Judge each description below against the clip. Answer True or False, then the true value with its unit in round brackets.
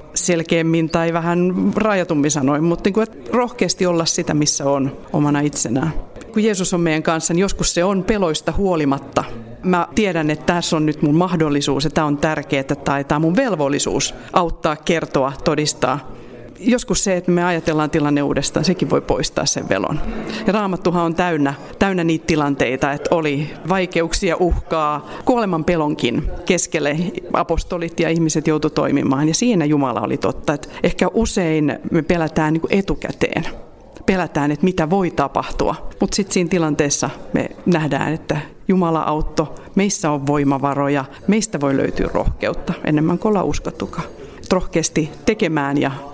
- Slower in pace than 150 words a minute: False (155 wpm)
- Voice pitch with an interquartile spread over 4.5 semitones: False (3.6 semitones)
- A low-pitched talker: False (165 Hz)